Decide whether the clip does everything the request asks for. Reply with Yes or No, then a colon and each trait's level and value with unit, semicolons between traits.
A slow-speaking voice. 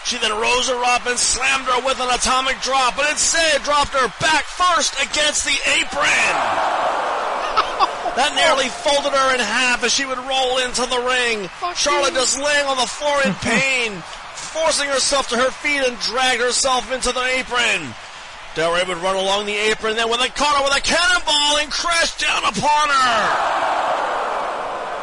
No: average, 175 wpm